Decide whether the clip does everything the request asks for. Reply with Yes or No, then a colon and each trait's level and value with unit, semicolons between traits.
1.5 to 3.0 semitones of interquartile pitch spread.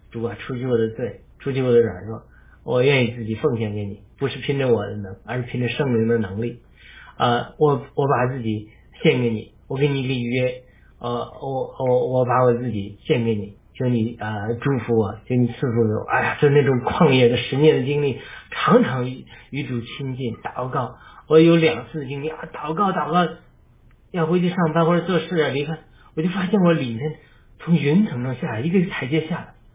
No: average, 4.7 semitones